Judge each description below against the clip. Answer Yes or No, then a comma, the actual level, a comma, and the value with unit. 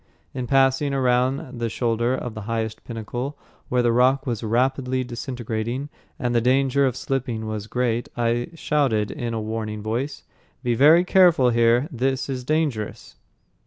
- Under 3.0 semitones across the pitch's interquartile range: Yes, narrow, 2.6 semitones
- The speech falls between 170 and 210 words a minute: No, average, 155 wpm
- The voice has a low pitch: Yes, low, 125 Hz